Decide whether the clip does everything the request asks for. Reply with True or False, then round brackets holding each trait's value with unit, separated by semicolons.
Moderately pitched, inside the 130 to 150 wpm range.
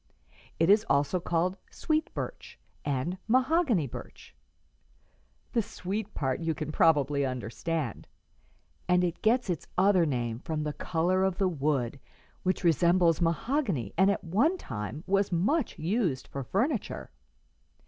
True (175 Hz; 140 wpm)